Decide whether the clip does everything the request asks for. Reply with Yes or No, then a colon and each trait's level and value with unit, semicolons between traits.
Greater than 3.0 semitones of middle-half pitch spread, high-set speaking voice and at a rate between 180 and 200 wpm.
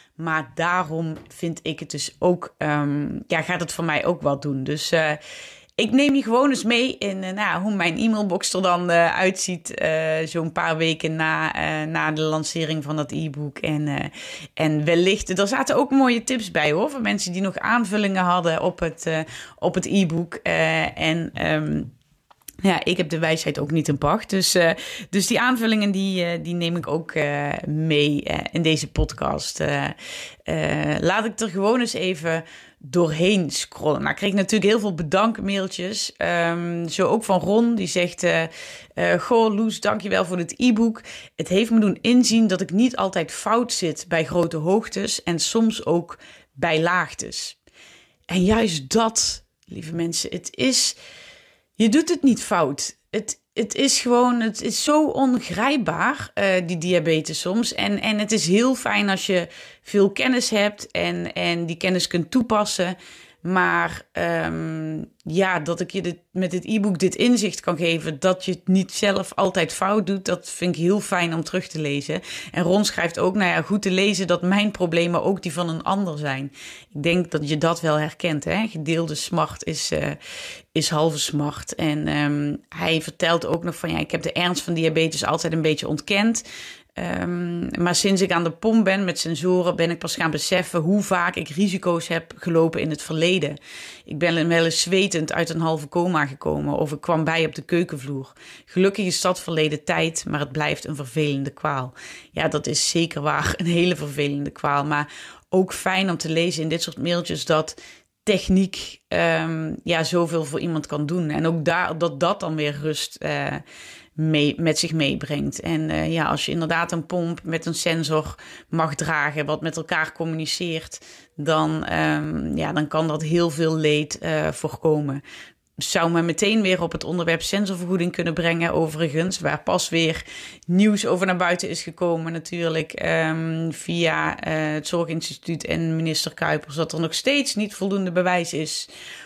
No: average, 3.4 semitones; medium, 170 Hz; average, 185 wpm